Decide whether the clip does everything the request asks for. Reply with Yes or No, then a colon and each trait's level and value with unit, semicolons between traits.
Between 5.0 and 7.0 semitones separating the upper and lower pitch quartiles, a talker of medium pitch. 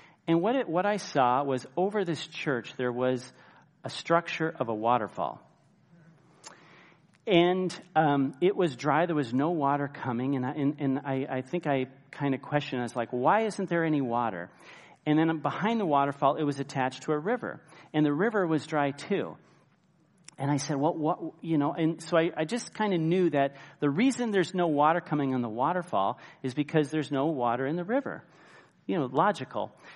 No: average, 4.2 semitones; medium, 150 Hz